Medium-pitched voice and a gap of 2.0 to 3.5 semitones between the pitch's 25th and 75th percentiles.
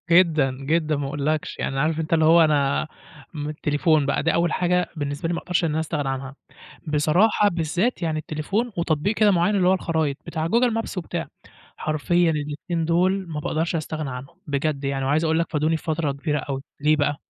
Yes: medium, 155 Hz; narrow, 2.6 semitones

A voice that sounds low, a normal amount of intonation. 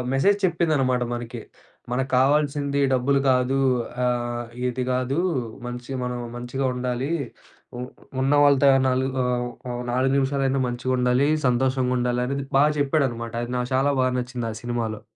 No: low, 130 Hz; narrow, 2.0 semitones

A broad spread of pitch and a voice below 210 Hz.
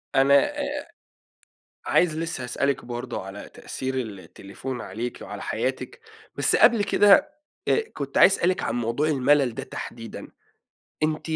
Yes: wide, 5.7 semitones; low, 135 Hz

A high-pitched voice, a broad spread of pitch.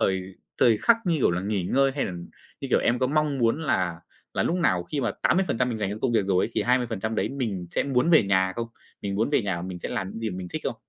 No: low, 115 Hz; wide, 6.2 semitones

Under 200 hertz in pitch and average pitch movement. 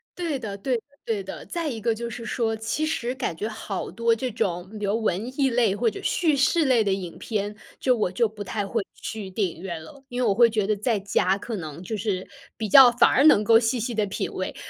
No: high, 220 Hz; average, 3.5 semitones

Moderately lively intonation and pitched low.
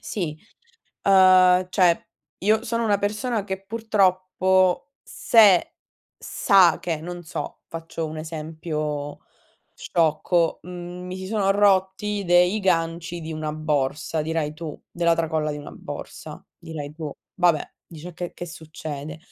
No: average, 3.3 semitones; medium, 175 Hz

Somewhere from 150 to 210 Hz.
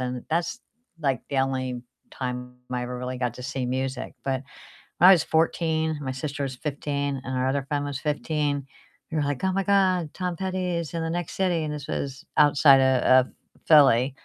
No: medium, 140 Hz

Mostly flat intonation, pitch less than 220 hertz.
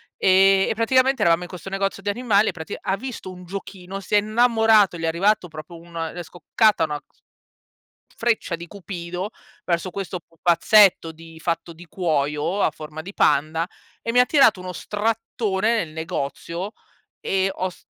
No: average, 3.8 semitones; medium, 185 Hz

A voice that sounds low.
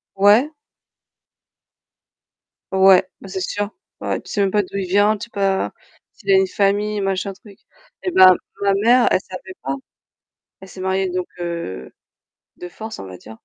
No: high, 195 Hz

